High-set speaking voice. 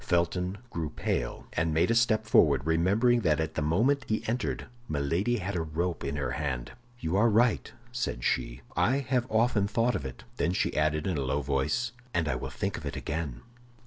No: very low, 85 Hz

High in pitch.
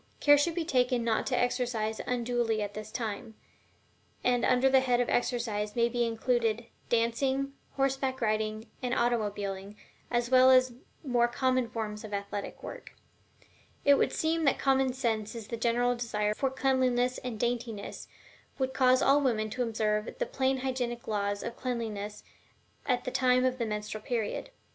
Yes: high, 240 Hz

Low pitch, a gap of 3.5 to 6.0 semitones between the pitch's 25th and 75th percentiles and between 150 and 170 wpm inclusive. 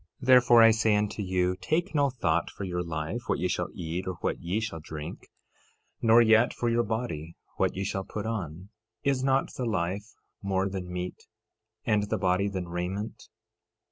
No: low, 100 Hz; average, 4.2 semitones; average, 180 wpm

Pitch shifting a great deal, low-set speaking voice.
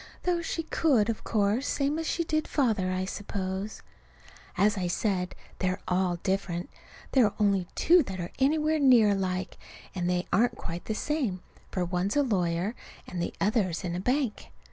No: wide, 6.1 semitones; high, 200 Hz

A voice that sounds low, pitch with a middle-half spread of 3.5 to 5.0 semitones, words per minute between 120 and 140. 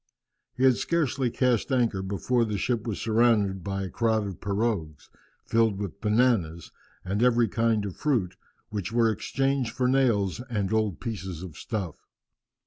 No: low, 110 Hz; average, 3.8 semitones; average, 155 wpm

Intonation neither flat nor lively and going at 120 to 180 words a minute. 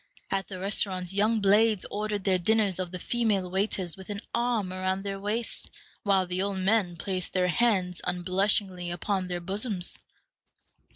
No: narrow, 2.2 semitones; average, 160 wpm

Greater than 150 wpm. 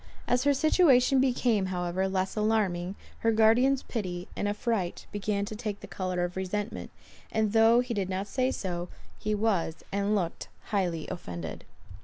Yes: average, 160 wpm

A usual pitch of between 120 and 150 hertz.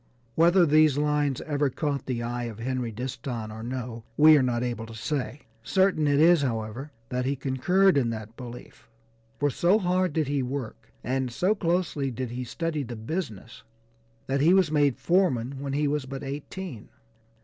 Yes: low, 135 Hz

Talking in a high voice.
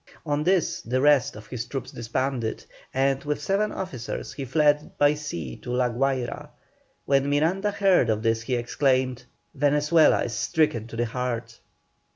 No: low, 135 Hz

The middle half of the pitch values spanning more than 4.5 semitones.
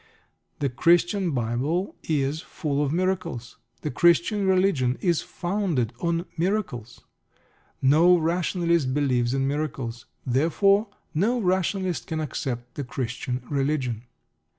Yes: wide, 5.6 semitones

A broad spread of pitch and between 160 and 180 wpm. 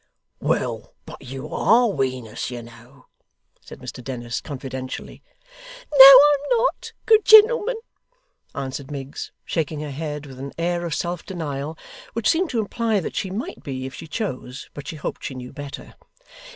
Yes: wide, 8.9 semitones; average, 165 wpm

